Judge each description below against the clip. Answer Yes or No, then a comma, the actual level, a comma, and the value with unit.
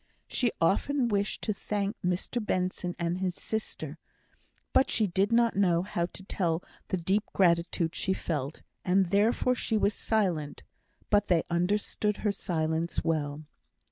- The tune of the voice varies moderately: Yes, average, 3.6 semitones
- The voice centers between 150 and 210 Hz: Yes, high, 190 Hz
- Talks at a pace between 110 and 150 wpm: Yes, average, 145 wpm